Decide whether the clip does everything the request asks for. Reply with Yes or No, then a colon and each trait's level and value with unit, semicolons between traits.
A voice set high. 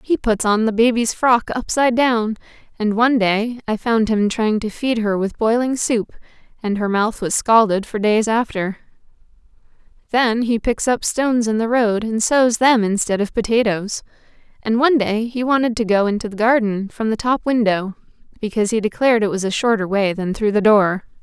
Yes: high, 220 Hz